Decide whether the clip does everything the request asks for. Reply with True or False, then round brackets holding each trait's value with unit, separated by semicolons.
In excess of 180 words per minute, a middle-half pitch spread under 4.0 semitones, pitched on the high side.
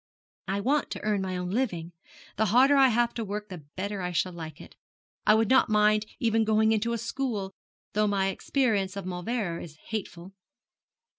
True (190 wpm; 3.4 semitones; 210 Hz)